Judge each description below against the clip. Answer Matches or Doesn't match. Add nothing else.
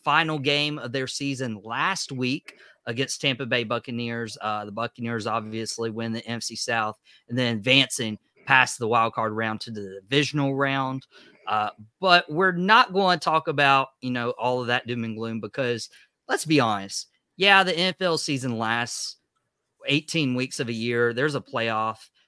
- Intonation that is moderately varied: Matches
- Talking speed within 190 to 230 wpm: Doesn't match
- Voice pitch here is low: Matches